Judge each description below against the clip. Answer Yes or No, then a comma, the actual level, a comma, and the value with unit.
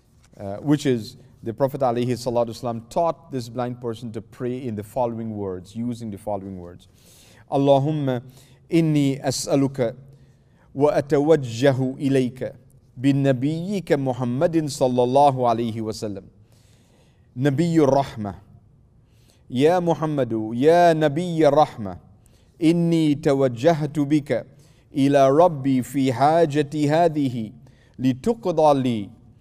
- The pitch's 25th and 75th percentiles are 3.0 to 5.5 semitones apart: Yes, average, 4.0 semitones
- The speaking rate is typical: No, slow, 95 wpm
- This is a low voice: Yes, low, 130 Hz